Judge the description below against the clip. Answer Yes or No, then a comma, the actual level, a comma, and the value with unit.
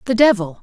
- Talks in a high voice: Yes, high, 215 Hz